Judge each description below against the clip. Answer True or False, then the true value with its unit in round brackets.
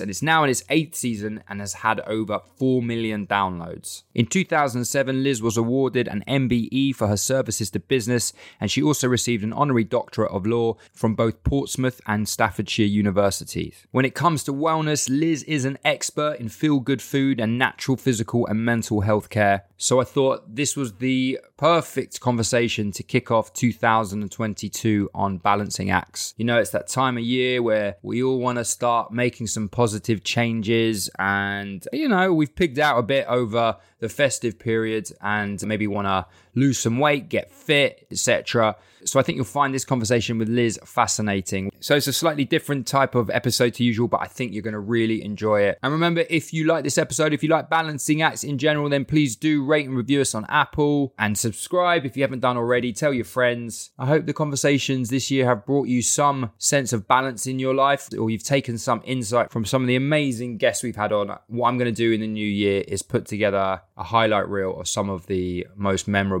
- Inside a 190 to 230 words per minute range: True (205 wpm)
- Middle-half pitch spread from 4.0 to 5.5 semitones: True (4.3 semitones)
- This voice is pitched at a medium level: False (120 Hz)